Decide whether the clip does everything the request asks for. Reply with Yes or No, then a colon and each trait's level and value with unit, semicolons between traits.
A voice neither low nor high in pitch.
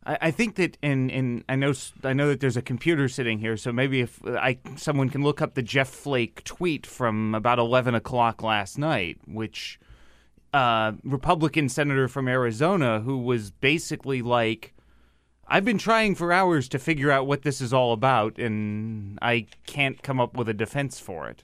No: low, 130 Hz